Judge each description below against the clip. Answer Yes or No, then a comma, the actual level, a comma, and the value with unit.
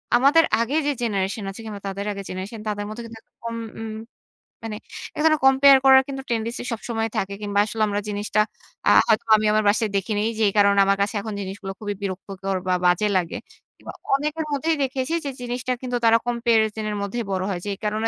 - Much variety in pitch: No, average, 3.3 semitones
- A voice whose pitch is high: Yes, high, 220 Hz